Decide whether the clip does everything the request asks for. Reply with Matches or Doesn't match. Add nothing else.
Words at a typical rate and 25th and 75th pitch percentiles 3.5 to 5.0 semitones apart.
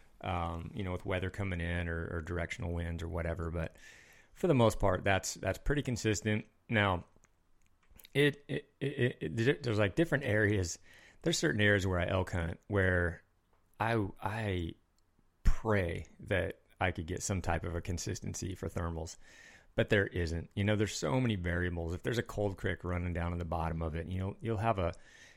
Matches